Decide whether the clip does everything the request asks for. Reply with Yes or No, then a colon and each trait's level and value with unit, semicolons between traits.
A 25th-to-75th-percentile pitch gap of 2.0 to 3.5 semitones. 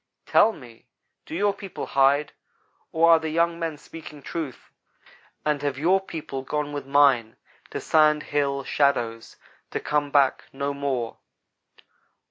Yes: narrow, 2.6 semitones